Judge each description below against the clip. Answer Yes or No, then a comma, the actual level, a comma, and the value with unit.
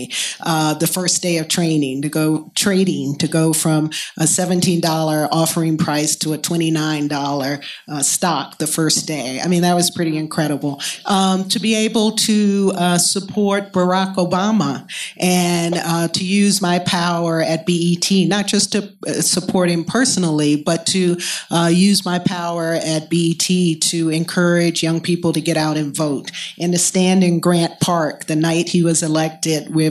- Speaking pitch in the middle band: Yes, medium, 170 Hz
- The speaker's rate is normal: Yes, average, 165 wpm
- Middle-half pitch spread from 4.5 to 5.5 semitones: No, narrow, 2.4 semitones